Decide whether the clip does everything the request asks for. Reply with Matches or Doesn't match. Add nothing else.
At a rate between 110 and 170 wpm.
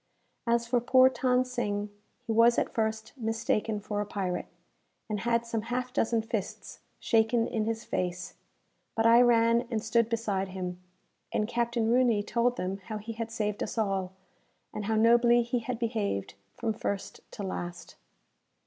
Matches